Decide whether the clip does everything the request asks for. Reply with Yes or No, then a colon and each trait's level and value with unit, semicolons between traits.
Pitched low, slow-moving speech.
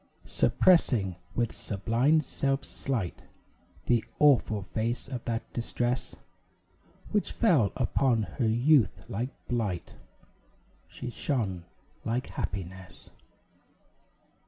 Yes: low, 120 Hz; slow, 90 wpm